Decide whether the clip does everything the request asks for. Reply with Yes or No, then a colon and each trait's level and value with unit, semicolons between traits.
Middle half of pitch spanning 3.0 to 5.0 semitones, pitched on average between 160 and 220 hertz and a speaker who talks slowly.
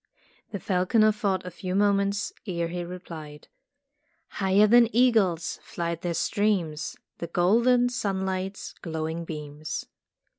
Yes: average, 3.5 semitones; medium, 185 Hz; slow, 120 wpm